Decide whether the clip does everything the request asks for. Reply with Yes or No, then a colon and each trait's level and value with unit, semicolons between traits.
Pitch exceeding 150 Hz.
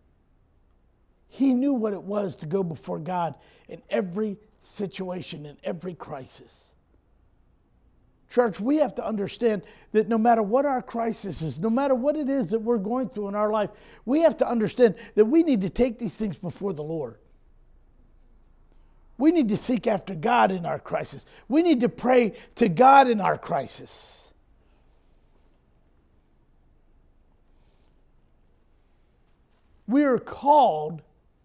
Yes: medium, 185 Hz